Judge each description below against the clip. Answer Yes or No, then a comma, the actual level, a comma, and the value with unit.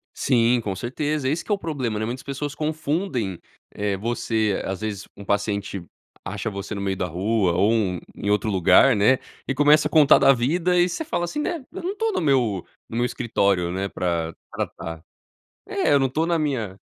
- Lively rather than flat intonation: Yes, wide, 7.1 semitones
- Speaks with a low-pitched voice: Yes, low, 115 Hz